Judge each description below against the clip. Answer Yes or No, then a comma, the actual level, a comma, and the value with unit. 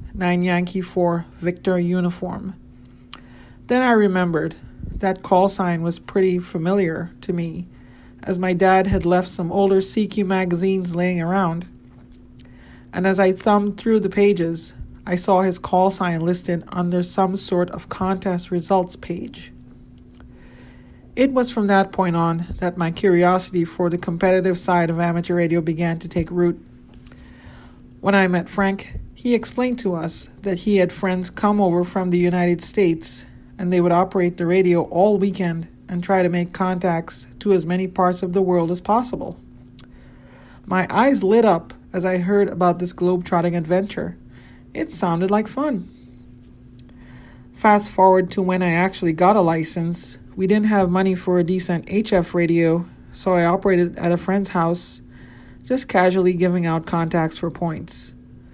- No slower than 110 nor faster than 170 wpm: Yes, average, 160 wpm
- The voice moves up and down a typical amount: No, narrow, 2.1 semitones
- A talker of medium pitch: Yes, medium, 180 Hz